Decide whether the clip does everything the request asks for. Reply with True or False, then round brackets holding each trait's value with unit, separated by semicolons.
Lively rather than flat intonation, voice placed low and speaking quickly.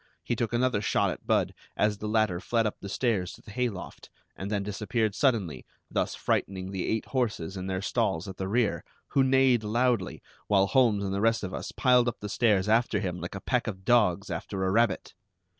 False (3.7 semitones; 105 Hz; 215 wpm)